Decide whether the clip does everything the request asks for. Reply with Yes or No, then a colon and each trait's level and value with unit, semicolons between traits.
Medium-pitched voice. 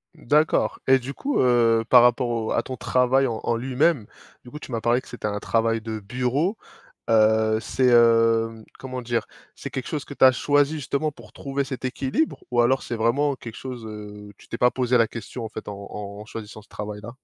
No: low, 120 Hz